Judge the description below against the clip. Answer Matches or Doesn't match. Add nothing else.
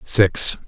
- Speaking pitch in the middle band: Doesn't match